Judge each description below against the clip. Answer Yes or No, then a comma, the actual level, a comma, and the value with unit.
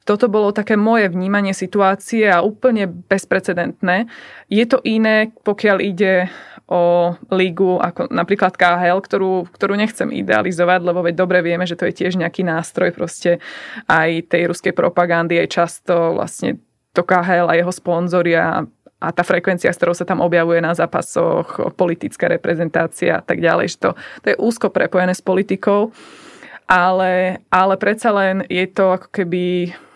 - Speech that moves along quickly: No, average, 155 wpm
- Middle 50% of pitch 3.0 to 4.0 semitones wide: No, narrow, 2.6 semitones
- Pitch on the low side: No, medium, 185 Hz